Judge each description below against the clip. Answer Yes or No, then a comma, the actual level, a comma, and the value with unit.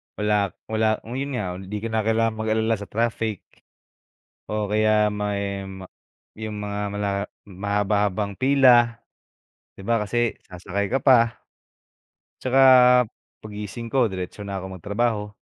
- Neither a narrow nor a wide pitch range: No, narrow, 2.2 semitones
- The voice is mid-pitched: No, low, 105 Hz